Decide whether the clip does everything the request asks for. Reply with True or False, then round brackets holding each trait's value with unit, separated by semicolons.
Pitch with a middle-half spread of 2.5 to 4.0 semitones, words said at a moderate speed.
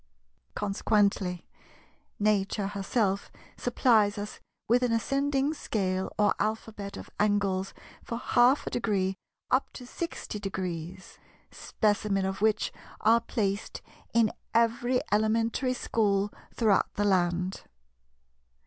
False (2.9 semitones; 105 wpm)